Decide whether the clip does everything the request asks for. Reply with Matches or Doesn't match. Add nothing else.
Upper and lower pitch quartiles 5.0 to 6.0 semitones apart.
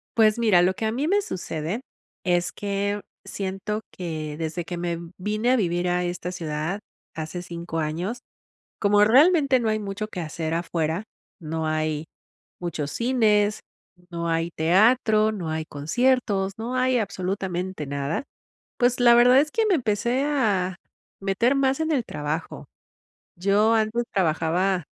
Matches